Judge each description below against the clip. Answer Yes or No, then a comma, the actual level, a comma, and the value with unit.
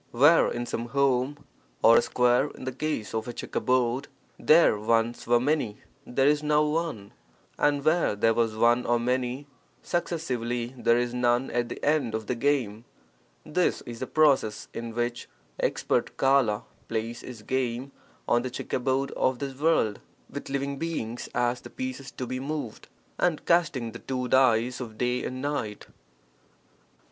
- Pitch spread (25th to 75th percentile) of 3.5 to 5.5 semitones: No, average, 3.0 semitones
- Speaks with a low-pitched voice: Yes, low, 125 Hz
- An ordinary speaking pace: Yes, average, 165 wpm